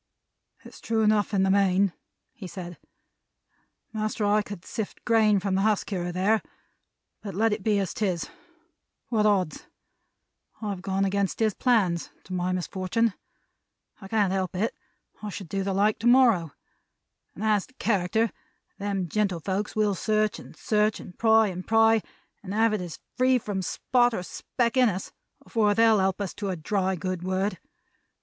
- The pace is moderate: Yes, average, 170 wpm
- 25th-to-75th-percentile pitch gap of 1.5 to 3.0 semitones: Yes, narrow, 2.6 semitones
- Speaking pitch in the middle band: No, high, 205 Hz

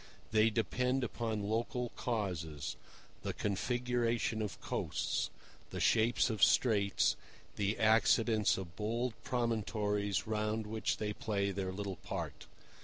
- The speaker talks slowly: Yes, slow, 110 wpm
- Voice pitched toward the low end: Yes, low, 110 Hz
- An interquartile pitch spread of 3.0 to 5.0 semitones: No, narrow, 2.5 semitones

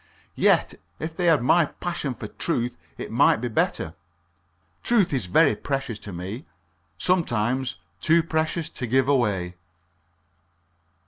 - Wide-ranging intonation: Yes, wide, 6.3 semitones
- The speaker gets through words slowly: Yes, slow, 130 wpm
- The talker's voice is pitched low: Yes, low, 130 Hz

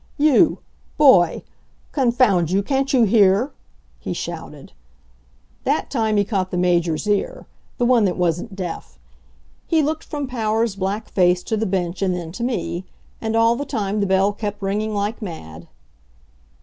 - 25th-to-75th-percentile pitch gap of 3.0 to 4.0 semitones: No, average, 4.7 semitones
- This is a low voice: No, high, 205 Hz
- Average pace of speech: Yes, average, 160 wpm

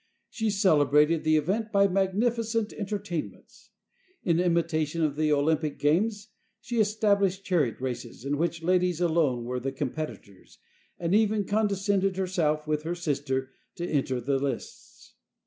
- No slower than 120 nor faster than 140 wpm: Yes, slow, 135 wpm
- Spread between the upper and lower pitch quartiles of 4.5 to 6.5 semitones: Yes, average, 5.2 semitones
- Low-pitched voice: No, medium, 170 Hz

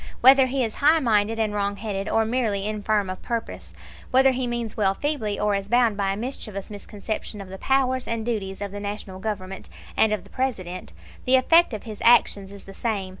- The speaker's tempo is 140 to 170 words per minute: No, average, 200 wpm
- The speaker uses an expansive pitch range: No, average, 3.4 semitones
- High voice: Yes, high, 215 Hz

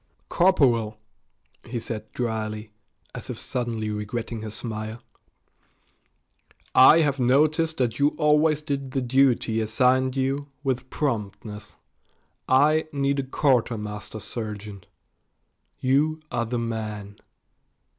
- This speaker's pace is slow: Yes, slow, 105 wpm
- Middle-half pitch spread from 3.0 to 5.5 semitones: Yes, average, 4.2 semitones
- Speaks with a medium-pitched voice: No, low, 125 Hz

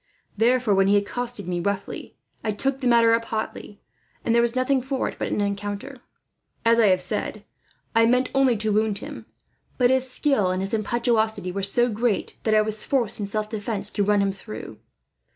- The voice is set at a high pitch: Yes, high, 220 Hz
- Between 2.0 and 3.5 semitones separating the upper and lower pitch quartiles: Yes, average, 3.2 semitones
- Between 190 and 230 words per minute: Yes, average, 200 wpm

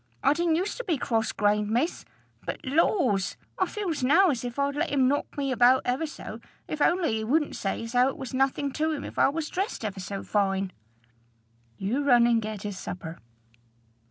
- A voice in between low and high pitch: No, very high, 260 Hz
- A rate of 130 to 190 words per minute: No, fast, 205 wpm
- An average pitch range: No, wide, 5.9 semitones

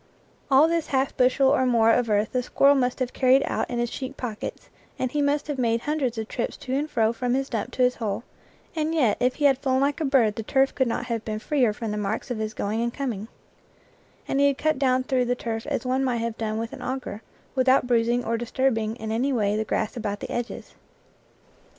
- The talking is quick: Yes, fast, 245 wpm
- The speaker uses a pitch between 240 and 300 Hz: Yes, very high, 250 Hz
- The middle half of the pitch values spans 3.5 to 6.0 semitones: No, average, 3.0 semitones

